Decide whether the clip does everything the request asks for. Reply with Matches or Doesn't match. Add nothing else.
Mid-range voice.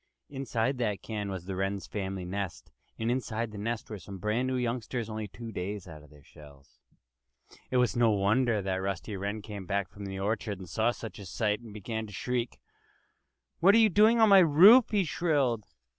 Doesn't match